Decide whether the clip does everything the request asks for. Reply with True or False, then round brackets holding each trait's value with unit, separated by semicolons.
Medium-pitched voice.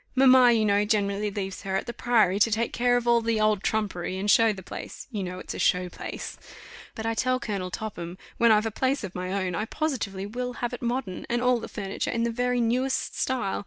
False (220 Hz)